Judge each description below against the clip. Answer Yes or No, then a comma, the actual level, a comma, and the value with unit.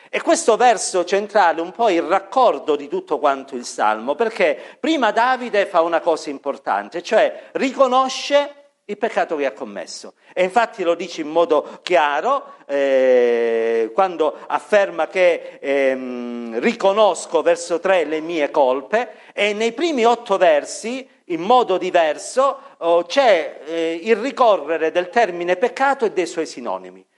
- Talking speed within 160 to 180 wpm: No, average, 145 wpm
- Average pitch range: No, wide, 8.2 semitones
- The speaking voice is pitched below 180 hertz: No, high, 200 Hz